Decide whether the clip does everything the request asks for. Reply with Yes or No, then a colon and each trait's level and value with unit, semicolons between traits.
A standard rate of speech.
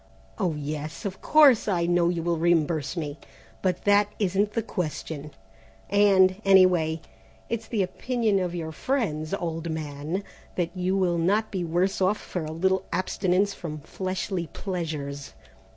Yes: average, 150 wpm